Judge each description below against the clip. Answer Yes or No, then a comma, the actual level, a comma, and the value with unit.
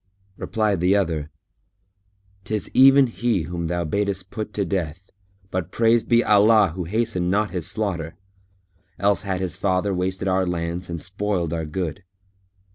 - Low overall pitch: Yes, very low, 95 Hz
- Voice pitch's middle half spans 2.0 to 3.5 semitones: Yes, average, 3.0 semitones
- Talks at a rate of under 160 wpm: Yes, average, 150 wpm